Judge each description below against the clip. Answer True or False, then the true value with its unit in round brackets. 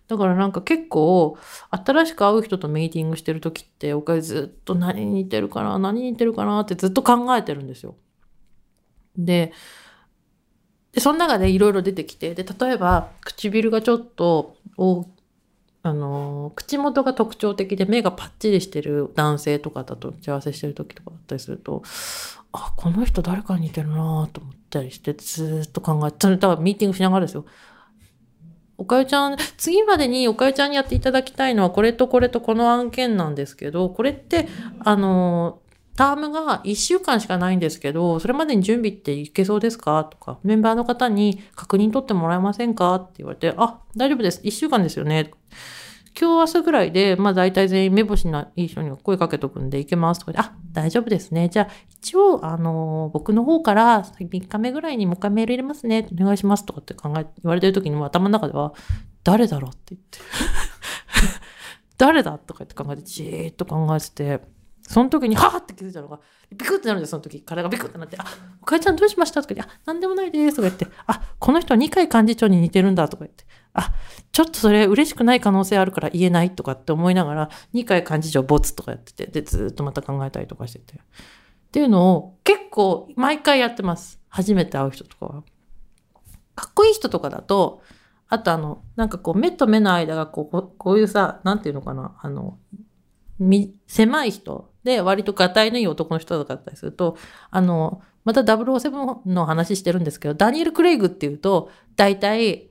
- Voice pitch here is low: False (190 Hz)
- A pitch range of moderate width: False (6.0 semitones)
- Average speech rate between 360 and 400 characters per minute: True (395 characters per minute)